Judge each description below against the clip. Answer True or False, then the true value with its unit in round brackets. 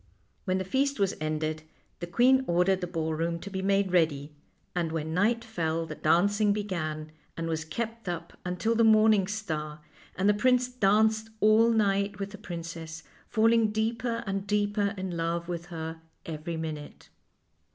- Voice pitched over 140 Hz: True (190 Hz)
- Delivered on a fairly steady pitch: False (4.7 semitones)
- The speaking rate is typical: True (160 wpm)